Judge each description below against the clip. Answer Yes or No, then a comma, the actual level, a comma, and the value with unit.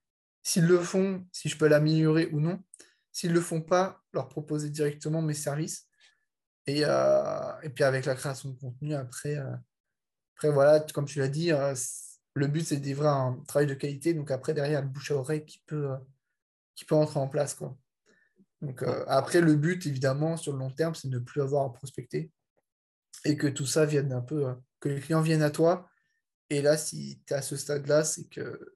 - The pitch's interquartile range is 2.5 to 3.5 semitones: Yes, average, 2.8 semitones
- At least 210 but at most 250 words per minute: Yes, average, 215 wpm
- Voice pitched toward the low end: No, medium, 150 Hz